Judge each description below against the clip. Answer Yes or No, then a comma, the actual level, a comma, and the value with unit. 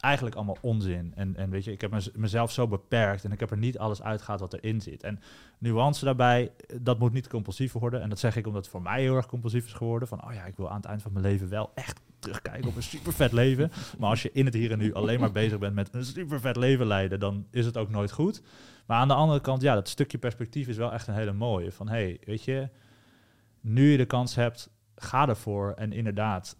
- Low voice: Yes, low, 115 Hz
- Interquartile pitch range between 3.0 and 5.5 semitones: Yes, average, 3.3 semitones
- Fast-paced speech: Yes, fast, 260 wpm